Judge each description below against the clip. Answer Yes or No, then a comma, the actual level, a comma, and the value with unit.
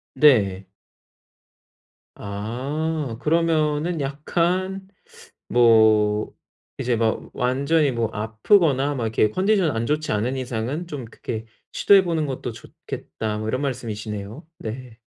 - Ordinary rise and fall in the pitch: No, wide, 5.8 semitones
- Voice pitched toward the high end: No, low, 130 Hz